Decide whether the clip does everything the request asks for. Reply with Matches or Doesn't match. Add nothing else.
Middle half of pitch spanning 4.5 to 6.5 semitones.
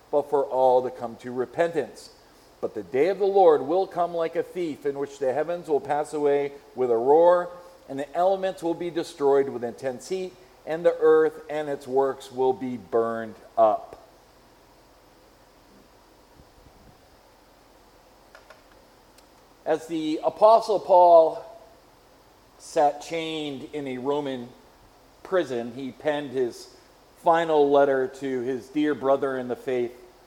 Matches